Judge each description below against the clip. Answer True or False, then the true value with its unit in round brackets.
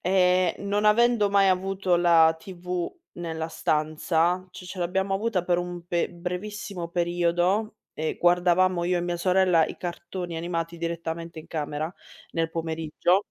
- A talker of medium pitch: True (175 Hz)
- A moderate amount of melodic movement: False (1.8 semitones)